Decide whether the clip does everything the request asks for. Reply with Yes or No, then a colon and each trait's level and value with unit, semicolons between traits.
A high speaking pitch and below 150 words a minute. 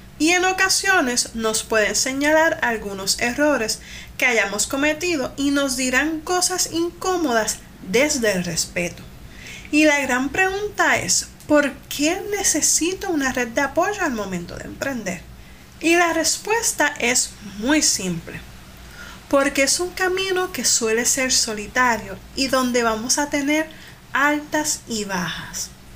Yes: very high, 280 Hz; average, 130 wpm